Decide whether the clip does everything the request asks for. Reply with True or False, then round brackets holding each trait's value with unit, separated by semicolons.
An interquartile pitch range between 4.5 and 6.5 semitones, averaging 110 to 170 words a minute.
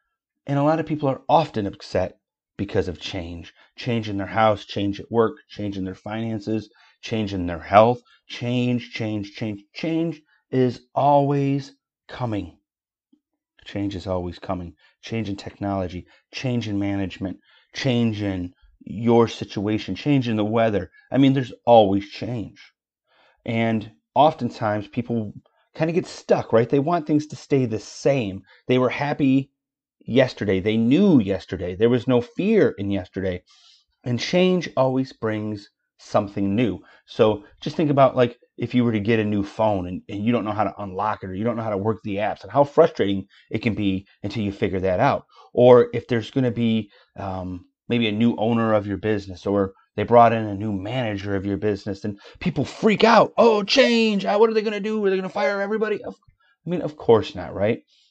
False (5.3 semitones; 185 wpm)